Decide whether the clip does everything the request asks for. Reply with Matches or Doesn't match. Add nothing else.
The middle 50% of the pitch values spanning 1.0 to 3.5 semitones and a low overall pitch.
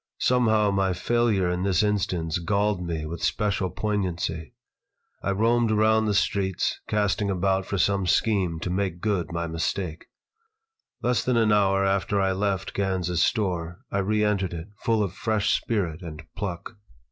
Matches